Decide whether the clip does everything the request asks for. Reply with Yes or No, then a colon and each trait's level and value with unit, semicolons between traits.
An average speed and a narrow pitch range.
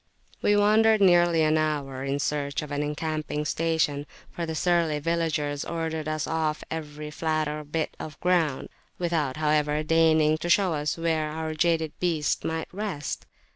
Yes: average, 155 wpm; narrow, 1.8 semitones